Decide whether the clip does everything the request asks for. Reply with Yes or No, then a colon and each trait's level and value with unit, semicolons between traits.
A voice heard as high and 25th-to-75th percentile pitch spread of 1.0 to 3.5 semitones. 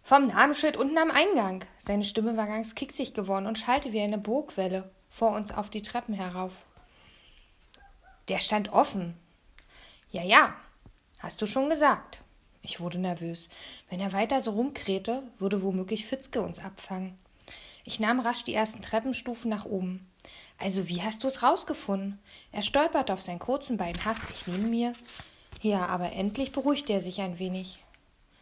No: high, 215 Hz; average, 4.5 semitones